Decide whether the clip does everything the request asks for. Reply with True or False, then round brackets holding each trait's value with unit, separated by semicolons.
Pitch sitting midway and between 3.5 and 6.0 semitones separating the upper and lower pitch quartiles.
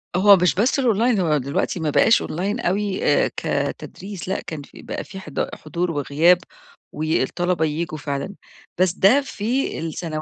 True (180 Hz; 4.5 semitones)